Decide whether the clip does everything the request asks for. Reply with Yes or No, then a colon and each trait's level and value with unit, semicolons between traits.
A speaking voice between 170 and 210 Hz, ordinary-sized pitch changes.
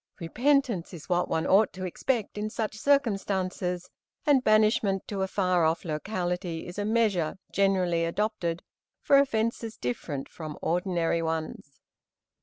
Yes: high, 190 Hz; average, 4.4 semitones